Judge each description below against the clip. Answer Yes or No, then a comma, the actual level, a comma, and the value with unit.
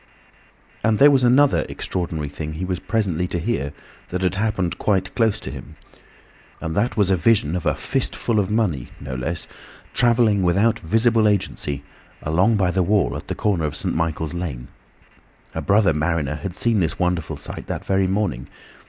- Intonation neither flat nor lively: Yes, average, 5.0 semitones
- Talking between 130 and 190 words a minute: Yes, average, 180 wpm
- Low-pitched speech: Yes, very low, 90 Hz